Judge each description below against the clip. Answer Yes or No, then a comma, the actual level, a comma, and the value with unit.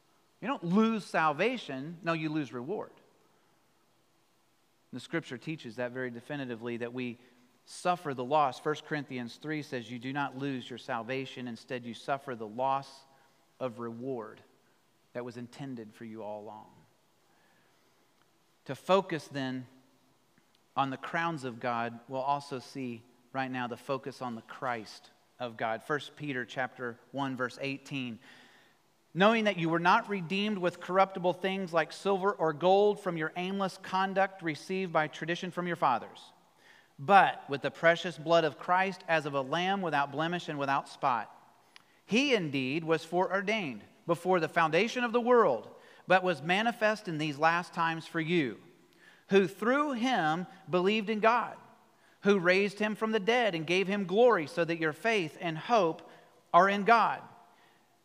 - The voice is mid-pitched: Yes, medium, 160 Hz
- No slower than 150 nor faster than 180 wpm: Yes, average, 160 wpm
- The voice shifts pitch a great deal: Yes, wide, 6.2 semitones